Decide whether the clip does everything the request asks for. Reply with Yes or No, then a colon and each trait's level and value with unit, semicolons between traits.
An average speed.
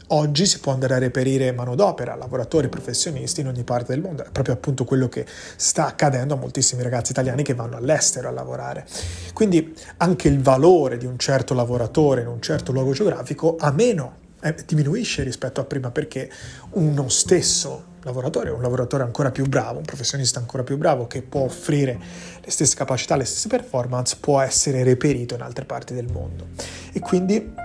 No: fast, 180 wpm